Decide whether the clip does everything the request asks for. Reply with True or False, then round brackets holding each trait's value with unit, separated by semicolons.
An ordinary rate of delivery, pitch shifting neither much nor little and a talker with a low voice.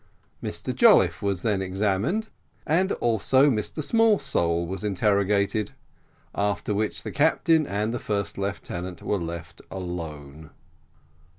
False (115 wpm; 4.8 semitones; 100 Hz)